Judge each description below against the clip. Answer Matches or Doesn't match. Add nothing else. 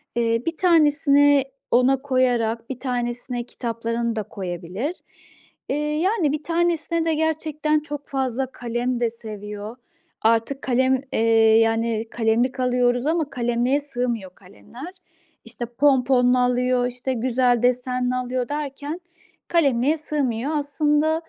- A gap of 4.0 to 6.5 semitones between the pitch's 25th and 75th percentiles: Doesn't match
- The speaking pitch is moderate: Doesn't match